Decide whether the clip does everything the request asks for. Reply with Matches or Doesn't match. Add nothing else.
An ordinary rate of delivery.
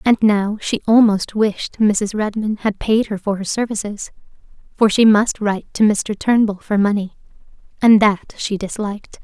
Matches